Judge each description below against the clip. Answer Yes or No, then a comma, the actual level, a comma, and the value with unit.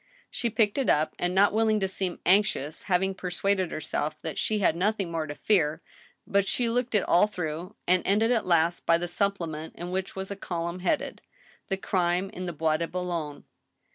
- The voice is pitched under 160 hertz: No, medium, 185 Hz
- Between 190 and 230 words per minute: Yes, average, 200 wpm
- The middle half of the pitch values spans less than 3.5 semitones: Yes, average, 3.1 semitones